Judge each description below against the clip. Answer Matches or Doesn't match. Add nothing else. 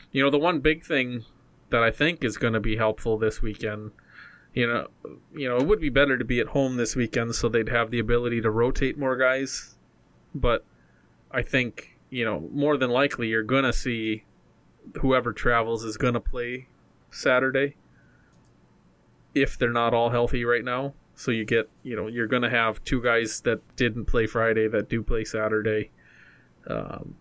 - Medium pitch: Doesn't match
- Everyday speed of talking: Matches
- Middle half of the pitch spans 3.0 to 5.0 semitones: Doesn't match